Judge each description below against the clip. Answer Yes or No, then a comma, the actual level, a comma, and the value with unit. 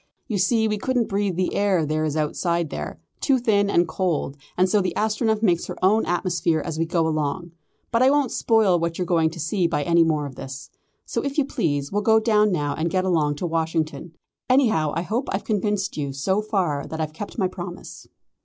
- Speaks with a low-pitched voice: No, medium, 180 Hz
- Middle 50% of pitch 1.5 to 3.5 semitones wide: No, average, 4.8 semitones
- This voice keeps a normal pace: No, fast, 220 wpm